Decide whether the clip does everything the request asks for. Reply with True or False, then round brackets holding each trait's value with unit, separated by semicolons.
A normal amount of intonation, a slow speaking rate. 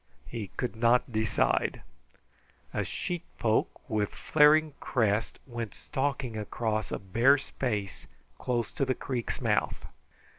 True (3.7 semitones; 115 wpm)